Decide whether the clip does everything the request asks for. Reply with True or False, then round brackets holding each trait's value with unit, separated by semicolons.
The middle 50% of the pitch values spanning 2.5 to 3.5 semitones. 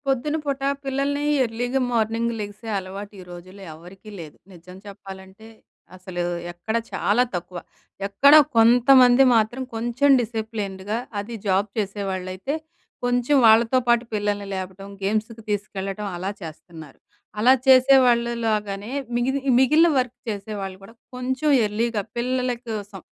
False (4.0 semitones)